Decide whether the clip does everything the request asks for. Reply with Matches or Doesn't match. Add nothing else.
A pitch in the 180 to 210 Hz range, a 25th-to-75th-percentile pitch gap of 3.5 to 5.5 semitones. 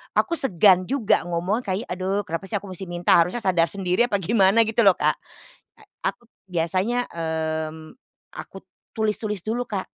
Matches